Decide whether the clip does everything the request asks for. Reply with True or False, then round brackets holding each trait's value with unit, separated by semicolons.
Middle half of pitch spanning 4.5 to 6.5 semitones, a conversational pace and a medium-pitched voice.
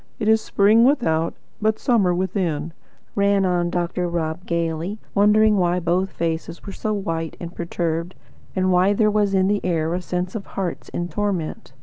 False (3.2 semitones; 170 wpm; 180 Hz)